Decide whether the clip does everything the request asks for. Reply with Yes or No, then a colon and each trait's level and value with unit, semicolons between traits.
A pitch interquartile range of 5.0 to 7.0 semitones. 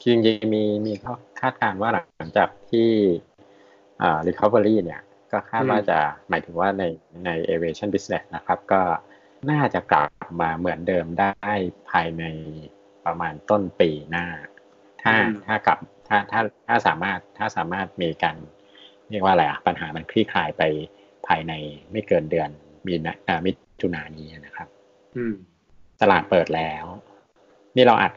No: average, 4.0 semitones